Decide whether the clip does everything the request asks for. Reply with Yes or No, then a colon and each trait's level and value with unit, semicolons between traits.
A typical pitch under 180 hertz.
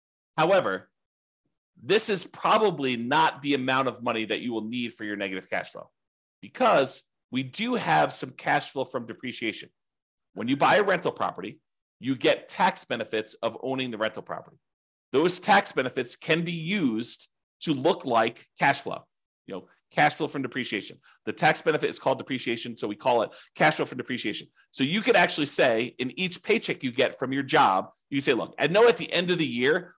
Yes: low, 135 Hz